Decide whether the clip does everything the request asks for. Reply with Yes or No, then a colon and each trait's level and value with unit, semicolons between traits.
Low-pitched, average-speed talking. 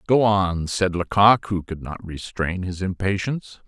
Yes: very low, 95 Hz; average, 165 wpm